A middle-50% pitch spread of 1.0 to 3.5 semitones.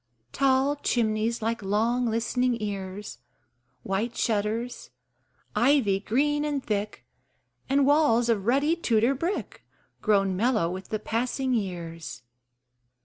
No: average, 4.3 semitones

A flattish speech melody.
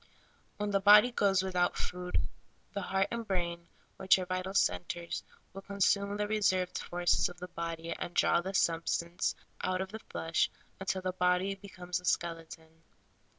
Yes: narrow, 2.3 semitones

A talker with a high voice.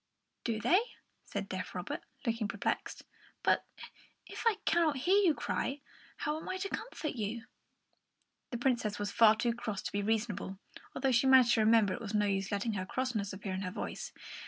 Yes: high, 230 Hz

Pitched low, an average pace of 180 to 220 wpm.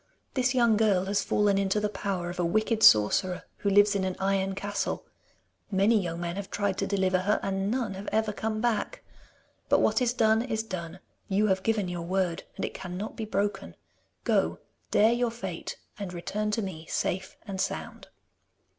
No: high, 200 Hz; average, 190 wpm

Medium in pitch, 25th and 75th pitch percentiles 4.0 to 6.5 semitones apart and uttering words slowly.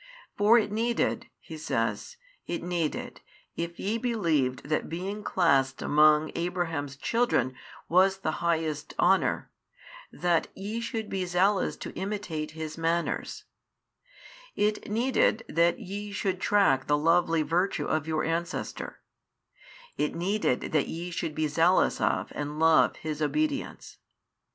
Yes: medium, 170 Hz; average, 4.5 semitones; slow, 130 wpm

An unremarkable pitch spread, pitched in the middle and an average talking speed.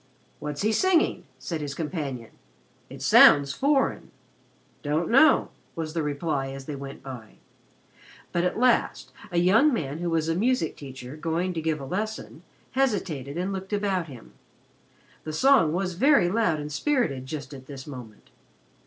No: wide, 6.0 semitones; medium, 160 Hz; average, 160 wpm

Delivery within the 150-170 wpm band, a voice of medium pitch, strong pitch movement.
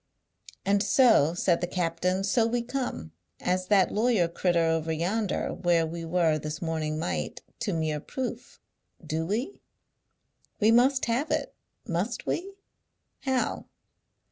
No: slow, 135 wpm; medium, 180 Hz; wide, 6.0 semitones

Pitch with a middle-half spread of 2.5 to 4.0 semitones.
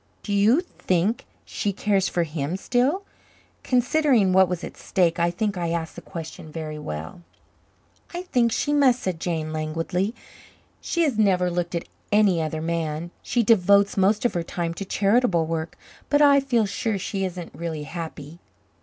No: average, 5.1 semitones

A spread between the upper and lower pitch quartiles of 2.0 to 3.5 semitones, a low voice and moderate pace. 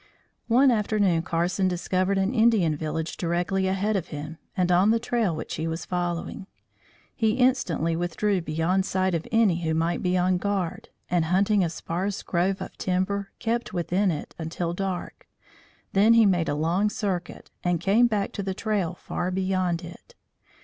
No: average, 2.9 semitones; medium, 185 Hz; average, 170 wpm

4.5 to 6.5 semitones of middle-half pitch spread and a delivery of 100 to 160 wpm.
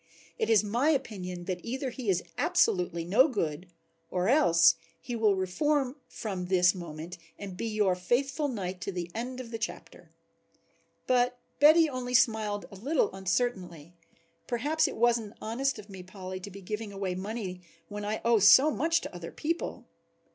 No: average, 5.3 semitones; average, 170 wpm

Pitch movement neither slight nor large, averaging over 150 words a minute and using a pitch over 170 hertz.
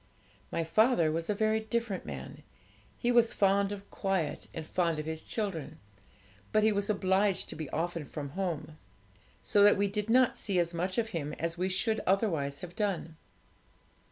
Yes: average, 4.2 semitones; average, 180 wpm; high, 190 Hz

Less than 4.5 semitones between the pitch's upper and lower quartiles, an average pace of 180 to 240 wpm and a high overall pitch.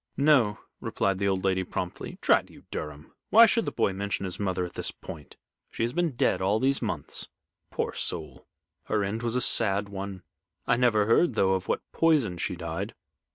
No: average, 4.1 semitones; average, 195 wpm; low, 100 Hz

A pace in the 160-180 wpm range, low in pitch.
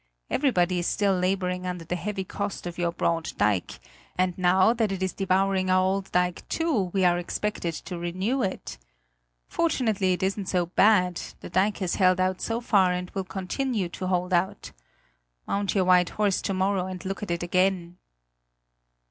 No: average, 175 wpm; medium, 185 Hz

